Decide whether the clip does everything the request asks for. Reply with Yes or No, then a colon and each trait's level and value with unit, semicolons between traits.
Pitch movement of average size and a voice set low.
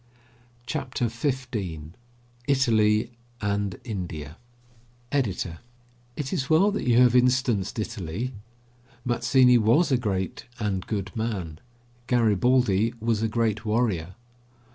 Yes: average, 3.8 semitones; low, 115 Hz